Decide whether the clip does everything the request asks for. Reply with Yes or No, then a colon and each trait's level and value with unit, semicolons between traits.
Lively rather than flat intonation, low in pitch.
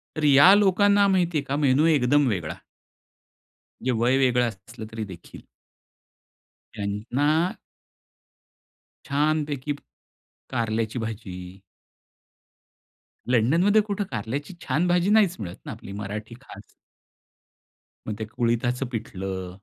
Yes: wide, 6.2 semitones; low, 125 Hz